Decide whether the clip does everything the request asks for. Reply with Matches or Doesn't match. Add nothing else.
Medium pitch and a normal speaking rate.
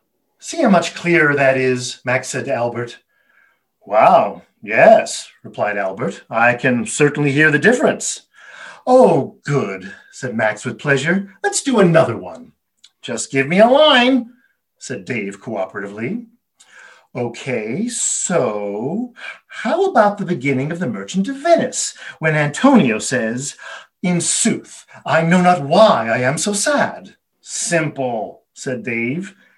Doesn't match